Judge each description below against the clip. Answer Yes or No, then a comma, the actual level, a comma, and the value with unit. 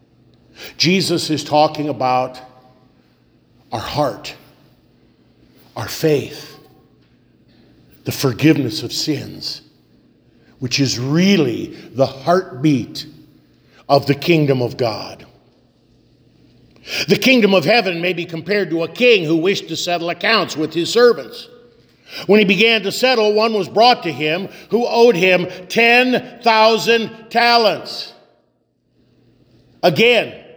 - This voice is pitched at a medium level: Yes, medium, 165 Hz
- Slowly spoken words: Yes, slow, 110 wpm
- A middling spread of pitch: No, wide, 7.7 semitones